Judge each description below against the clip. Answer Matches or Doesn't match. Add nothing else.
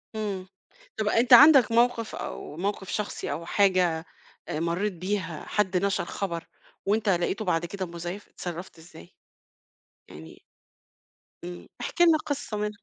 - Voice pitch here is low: Doesn't match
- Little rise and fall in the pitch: Doesn't match